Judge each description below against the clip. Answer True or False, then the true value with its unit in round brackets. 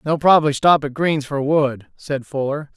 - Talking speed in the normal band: True (195 wpm)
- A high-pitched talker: False (145 Hz)